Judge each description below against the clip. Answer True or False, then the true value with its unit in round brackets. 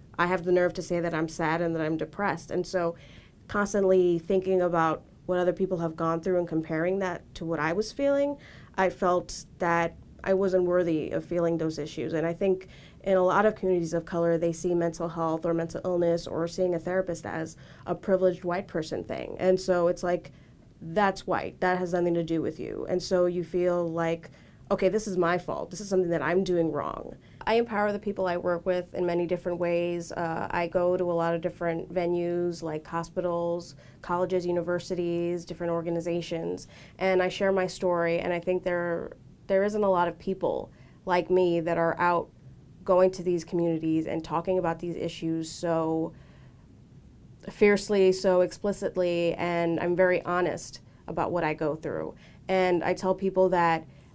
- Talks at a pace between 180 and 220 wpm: True (190 wpm)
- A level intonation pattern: True (1.7 semitones)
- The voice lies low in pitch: False (175 Hz)